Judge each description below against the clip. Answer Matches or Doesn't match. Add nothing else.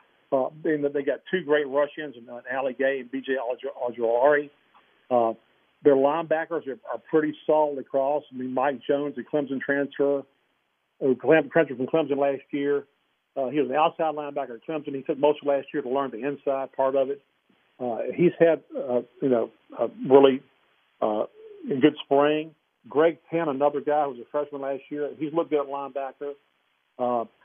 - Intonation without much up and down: Matches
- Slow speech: Doesn't match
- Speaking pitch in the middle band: Matches